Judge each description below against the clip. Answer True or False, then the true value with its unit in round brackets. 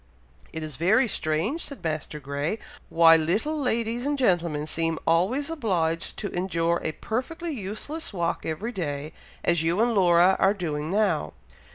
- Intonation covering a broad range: True (5.9 semitones)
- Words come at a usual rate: True (155 wpm)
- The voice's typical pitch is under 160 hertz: False (175 Hz)